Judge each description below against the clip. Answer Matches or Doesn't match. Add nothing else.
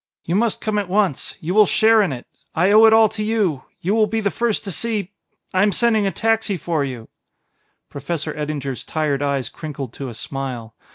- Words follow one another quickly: Matches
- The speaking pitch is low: Doesn't match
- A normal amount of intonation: Doesn't match